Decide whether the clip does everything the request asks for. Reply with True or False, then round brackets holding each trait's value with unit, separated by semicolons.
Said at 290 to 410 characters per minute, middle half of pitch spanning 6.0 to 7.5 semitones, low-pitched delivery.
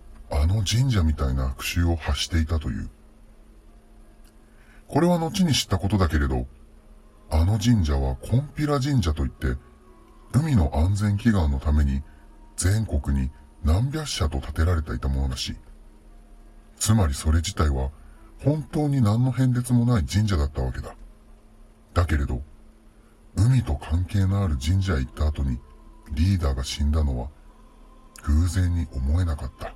False (280 characters per minute; 6.8 semitones; 85 Hz)